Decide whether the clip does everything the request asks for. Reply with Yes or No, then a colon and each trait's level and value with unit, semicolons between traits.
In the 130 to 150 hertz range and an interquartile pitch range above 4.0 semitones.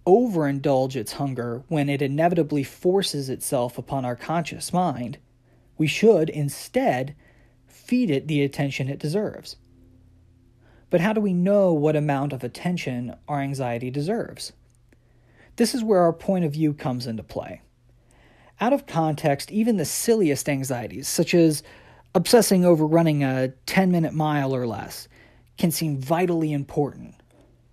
Yes: medium, 140 Hz; average, 5.3 semitones